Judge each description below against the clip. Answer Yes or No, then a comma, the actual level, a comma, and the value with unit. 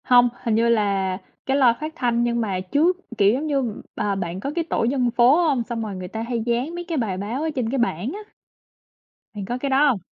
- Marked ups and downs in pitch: No, average, 4.6 semitones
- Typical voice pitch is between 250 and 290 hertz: No, high, 240 Hz